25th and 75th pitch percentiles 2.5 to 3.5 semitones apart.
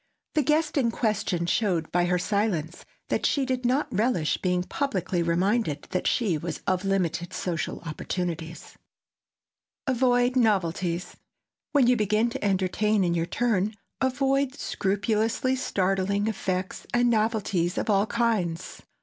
No: average, 5.1 semitones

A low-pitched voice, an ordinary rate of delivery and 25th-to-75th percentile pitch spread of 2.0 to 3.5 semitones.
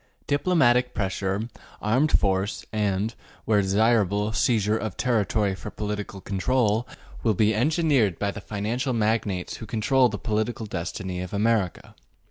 No: low, 105 Hz; slow, 130 wpm; average, 2.7 semitones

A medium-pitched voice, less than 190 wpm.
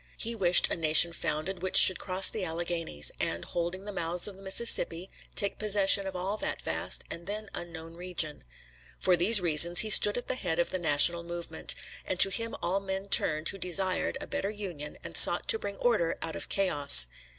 No: medium, 180 Hz; average, 200 wpm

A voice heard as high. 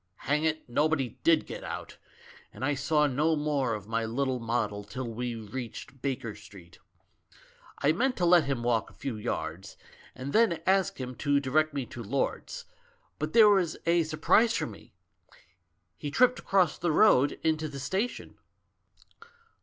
No: medium, 140 Hz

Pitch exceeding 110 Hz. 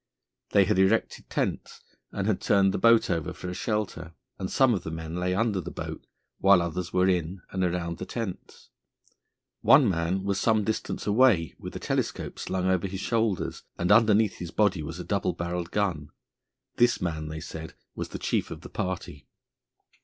No: very low, 95 Hz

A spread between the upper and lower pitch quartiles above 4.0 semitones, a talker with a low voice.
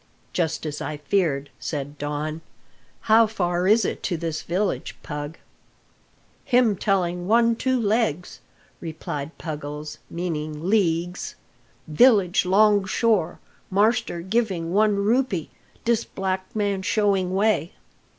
No: average, 5.0 semitones; medium, 185 Hz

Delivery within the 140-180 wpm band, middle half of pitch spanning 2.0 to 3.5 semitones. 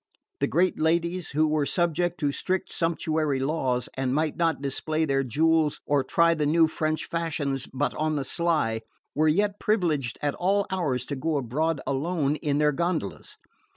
Yes: average, 170 wpm; average, 3.1 semitones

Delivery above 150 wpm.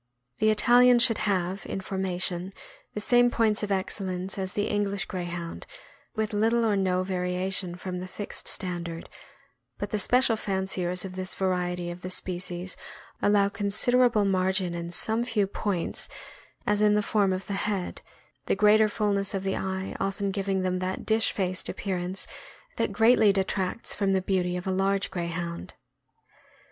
Yes: average, 160 wpm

